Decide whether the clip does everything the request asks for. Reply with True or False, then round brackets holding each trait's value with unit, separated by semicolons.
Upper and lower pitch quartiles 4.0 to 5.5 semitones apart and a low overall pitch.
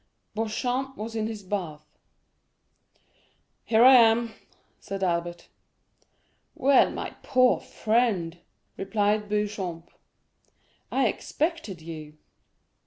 False (4.8 semitones; 210 Hz)